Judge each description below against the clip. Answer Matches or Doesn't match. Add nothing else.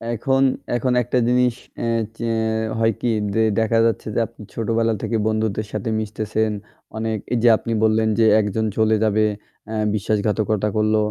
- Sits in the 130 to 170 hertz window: Doesn't match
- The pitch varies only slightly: Matches